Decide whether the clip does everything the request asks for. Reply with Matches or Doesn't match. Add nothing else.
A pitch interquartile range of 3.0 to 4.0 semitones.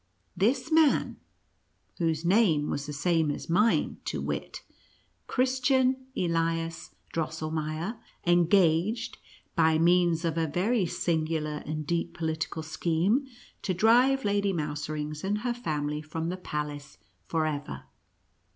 Doesn't match